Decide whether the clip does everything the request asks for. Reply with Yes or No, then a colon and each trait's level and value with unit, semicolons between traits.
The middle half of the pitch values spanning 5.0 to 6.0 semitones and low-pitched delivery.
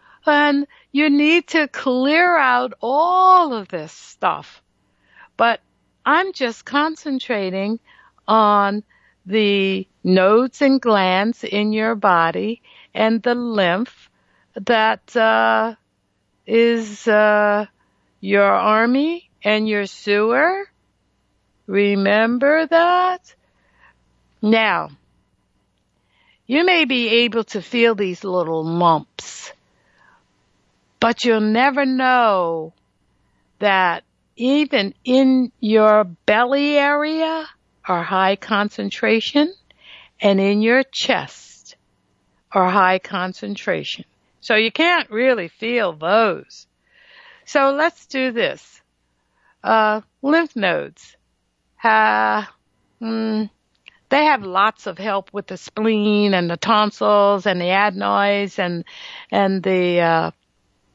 No: wide, 5.5 semitones; high, 215 Hz